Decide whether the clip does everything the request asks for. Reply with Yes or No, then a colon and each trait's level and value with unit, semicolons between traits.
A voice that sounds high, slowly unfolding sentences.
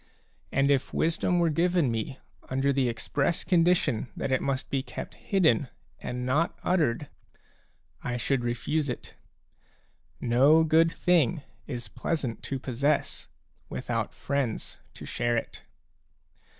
No: medium, 140 Hz; slow, 125 wpm